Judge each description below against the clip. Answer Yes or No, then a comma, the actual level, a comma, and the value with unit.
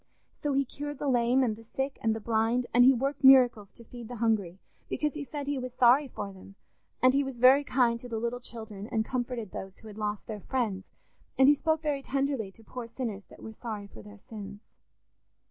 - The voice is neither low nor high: No, high, 240 Hz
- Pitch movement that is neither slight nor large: Yes, average, 3.5 semitones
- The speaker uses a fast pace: Yes, fast, 225 wpm